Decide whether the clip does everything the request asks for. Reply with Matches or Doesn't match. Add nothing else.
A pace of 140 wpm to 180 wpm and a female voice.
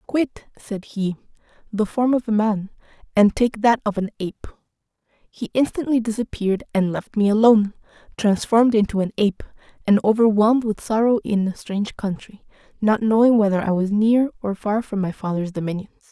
Matches